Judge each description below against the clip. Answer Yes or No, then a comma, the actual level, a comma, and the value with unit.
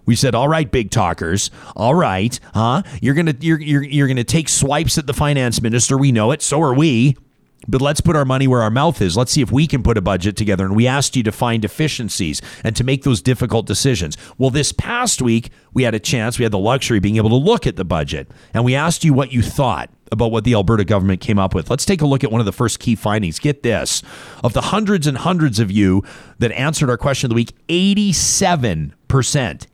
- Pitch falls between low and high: No, low, 125 Hz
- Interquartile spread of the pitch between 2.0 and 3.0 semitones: No, average, 4.5 semitones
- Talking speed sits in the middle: No, fast, 245 wpm